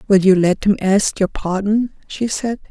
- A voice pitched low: No, high, 200 Hz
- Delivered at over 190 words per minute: Yes, average, 200 wpm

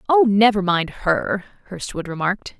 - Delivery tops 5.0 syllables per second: No, 4.7 syllables/s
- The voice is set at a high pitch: Yes, high, 200 Hz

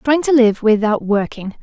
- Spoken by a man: No, female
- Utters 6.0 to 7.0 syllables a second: No, 4.7 syllables/s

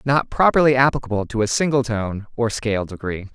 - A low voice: Yes, low, 120 Hz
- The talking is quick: No, average, 180 wpm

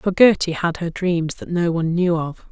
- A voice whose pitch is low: No, medium, 170 Hz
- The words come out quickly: Yes, fast, 240 wpm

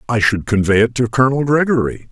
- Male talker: Yes, male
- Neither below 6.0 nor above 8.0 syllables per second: Yes, 6.2 syllables/s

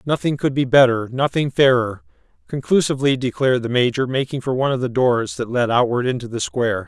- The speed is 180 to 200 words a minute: Yes, average, 185 wpm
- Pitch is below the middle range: Yes, low, 125 Hz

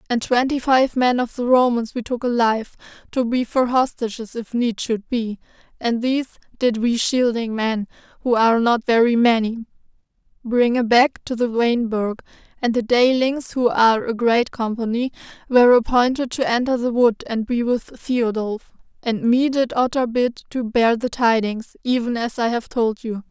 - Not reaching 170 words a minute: No, average, 175 wpm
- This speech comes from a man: No, female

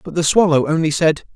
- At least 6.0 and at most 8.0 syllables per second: Yes, 6.1 syllables/s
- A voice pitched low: No, medium, 160 Hz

